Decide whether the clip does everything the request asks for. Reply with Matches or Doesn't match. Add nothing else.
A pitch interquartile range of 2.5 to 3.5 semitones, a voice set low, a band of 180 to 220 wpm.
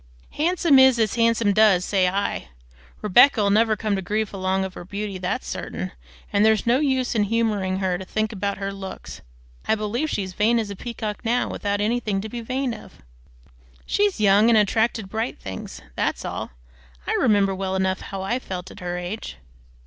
Doesn't match